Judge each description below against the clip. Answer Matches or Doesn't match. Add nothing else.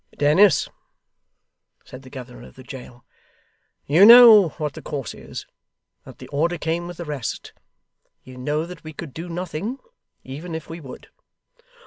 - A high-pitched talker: Doesn't match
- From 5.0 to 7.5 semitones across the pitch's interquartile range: Doesn't match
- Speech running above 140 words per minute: Matches